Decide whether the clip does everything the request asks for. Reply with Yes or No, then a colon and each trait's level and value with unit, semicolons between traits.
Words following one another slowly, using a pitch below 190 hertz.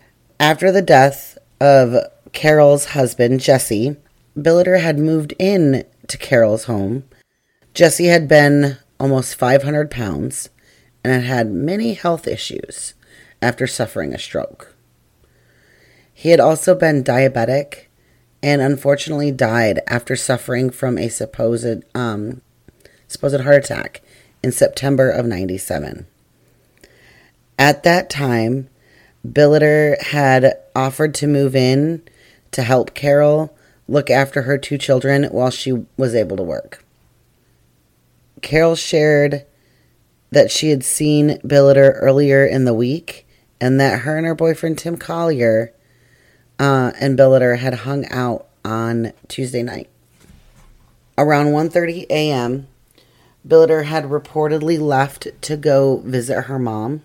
Yes: slow, 120 wpm; low, 135 Hz